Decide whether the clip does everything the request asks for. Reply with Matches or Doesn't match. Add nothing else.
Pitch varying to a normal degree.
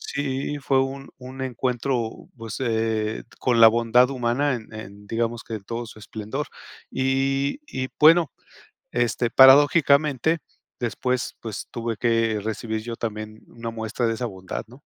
Matches